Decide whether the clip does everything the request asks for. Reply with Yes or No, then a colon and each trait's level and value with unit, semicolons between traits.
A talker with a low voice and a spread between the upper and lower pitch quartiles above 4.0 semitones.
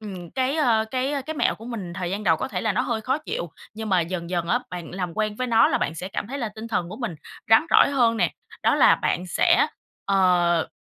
No: high, 215 Hz; average, 5.3 semitones